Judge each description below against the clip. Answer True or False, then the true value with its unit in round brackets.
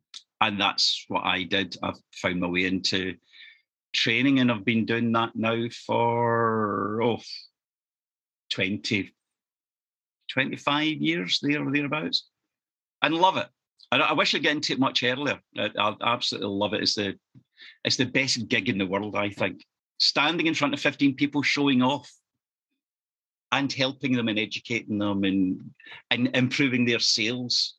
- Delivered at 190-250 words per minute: False (155 wpm)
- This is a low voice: True (115 Hz)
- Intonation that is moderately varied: True (5.0 semitones)